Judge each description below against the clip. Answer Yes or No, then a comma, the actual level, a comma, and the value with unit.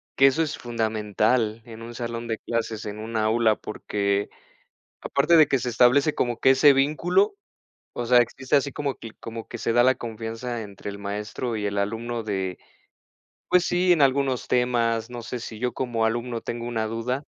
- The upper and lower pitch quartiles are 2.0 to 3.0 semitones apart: Yes, average, 2.7 semitones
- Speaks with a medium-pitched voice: No, low, 120 Hz